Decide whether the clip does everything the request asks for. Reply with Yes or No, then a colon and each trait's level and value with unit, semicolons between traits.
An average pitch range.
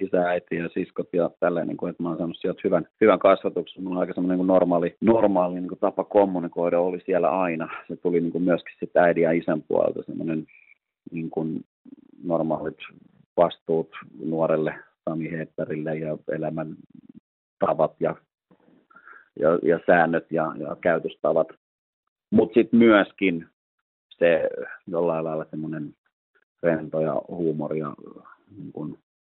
No: narrow, 2.3 semitones